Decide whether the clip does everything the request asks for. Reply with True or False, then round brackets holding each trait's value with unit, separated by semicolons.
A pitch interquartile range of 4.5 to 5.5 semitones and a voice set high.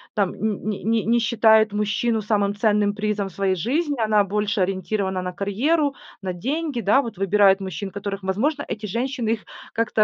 False (2.7 semitones; 210 Hz)